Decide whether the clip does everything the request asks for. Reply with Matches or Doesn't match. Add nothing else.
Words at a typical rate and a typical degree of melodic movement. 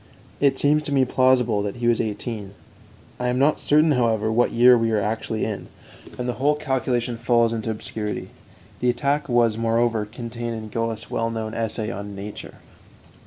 Doesn't match